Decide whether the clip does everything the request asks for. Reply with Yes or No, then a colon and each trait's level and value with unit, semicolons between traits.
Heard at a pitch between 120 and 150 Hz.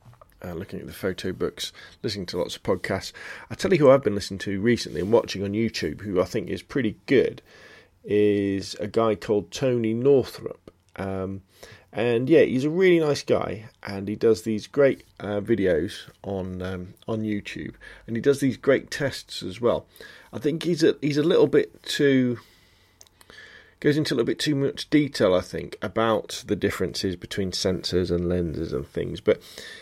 No: low, 105 Hz